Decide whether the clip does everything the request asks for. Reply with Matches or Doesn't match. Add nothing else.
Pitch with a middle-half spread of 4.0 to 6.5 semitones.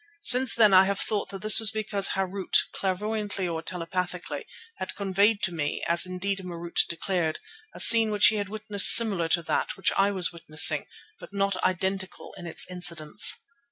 Doesn't match